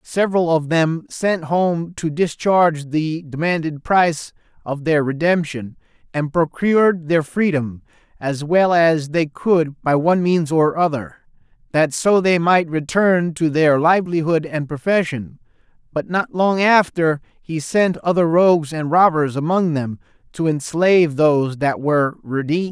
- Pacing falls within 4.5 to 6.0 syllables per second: No, 4.3 syllables/s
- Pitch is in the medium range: Yes, medium, 160 Hz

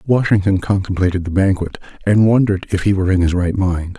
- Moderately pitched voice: No, very low, 95 Hz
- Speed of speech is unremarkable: Yes, average, 195 wpm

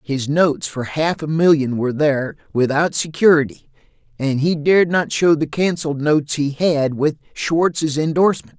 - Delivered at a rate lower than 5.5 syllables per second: Yes, 4.9 syllables/s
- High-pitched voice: No, medium, 150 Hz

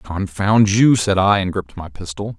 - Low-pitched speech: Yes, low, 100 Hz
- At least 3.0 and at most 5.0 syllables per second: Yes, 4.7 syllables/s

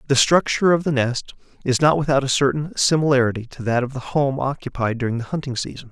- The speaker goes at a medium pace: No, fast, 215 wpm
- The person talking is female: No, male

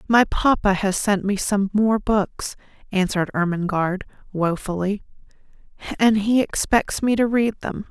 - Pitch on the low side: No, high, 205 Hz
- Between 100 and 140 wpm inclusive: Yes, slow, 135 wpm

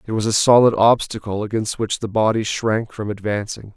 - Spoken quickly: No, average, 190 wpm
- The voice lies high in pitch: No, low, 110 Hz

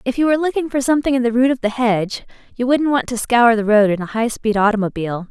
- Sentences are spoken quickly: Yes, fast, 260 wpm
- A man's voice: No, female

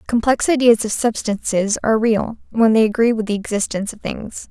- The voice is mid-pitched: No, high, 220 Hz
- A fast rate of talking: No, average, 185 wpm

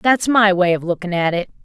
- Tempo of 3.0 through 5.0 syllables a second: No, 5.4 syllables/s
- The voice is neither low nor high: No, high, 195 Hz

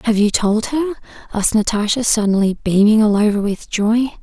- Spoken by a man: No, female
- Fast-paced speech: No, average, 170 wpm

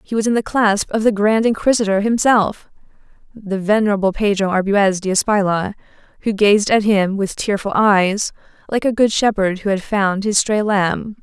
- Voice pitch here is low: No, high, 205 Hz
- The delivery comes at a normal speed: Yes, average, 170 wpm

